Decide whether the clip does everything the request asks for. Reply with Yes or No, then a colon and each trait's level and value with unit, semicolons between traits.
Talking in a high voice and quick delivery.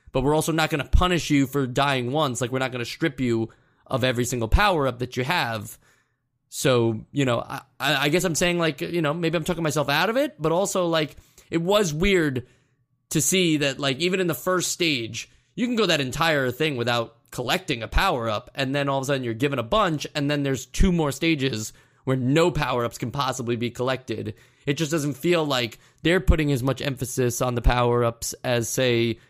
No: medium, 140 Hz; fast, 215 wpm